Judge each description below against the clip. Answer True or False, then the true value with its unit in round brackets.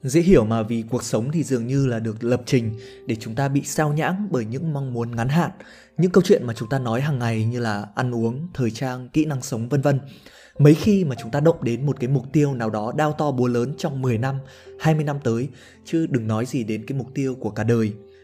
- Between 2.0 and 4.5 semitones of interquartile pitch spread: True (4.1 semitones)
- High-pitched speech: False (130 Hz)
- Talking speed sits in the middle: False (260 wpm)